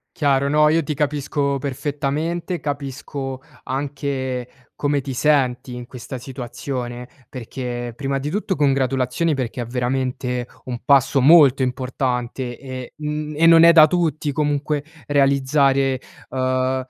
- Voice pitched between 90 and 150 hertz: Yes, low, 135 Hz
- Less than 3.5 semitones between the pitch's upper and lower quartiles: Yes, narrow, 2.5 semitones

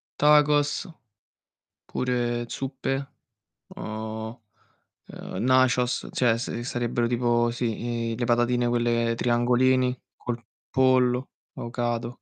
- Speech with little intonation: Yes, narrow, 1.4 semitones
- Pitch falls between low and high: No, low, 120 Hz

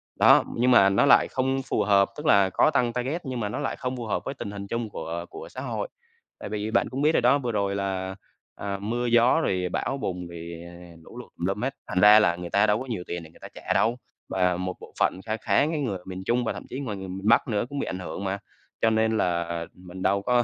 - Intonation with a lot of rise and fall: No, average, 4.5 semitones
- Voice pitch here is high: No, low, 105 Hz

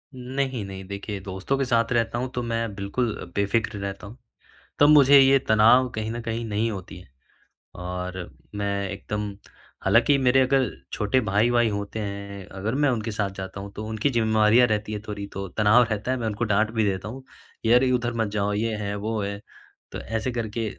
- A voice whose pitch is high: No, low, 110 Hz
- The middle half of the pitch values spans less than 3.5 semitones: Yes, average, 2.9 semitones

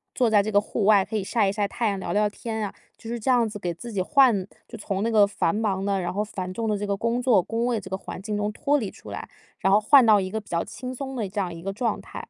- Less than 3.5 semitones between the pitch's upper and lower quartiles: Yes, average, 2.9 semitones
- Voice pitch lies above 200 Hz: Yes, high, 210 Hz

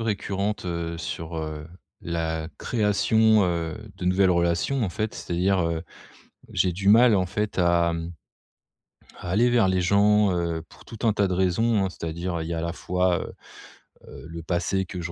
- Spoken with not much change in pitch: No, average, 3.3 semitones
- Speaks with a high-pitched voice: No, very low, 90 Hz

